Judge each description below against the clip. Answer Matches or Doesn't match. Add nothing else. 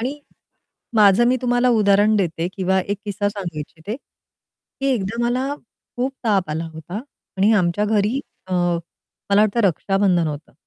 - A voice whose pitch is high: Matches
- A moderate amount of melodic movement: Matches